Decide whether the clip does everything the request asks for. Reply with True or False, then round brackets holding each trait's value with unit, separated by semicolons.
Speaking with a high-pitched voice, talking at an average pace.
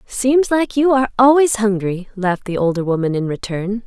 True (220 Hz; 185 wpm)